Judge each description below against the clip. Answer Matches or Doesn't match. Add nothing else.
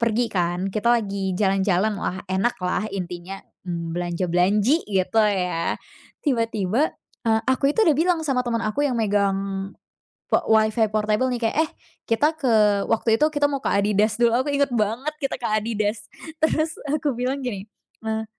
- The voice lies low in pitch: Doesn't match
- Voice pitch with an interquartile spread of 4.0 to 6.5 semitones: Matches